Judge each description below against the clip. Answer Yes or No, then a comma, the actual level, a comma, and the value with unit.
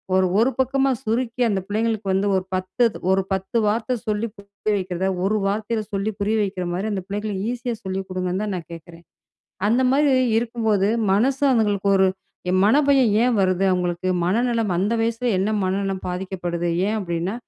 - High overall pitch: Yes, high, 205 Hz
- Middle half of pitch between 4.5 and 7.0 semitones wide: No, average, 3.4 semitones